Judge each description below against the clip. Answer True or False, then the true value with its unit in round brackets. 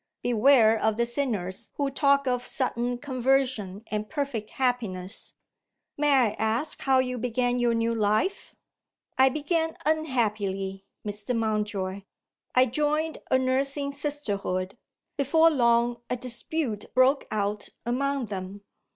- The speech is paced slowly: True (125 wpm)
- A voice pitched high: True (245 Hz)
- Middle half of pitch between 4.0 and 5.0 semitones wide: True (4.6 semitones)